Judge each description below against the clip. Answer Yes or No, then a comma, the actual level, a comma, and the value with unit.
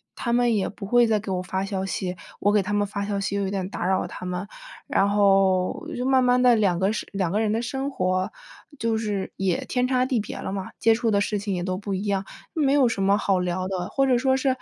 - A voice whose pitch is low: No, high, 205 Hz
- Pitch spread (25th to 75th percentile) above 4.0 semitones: No, average, 3.7 semitones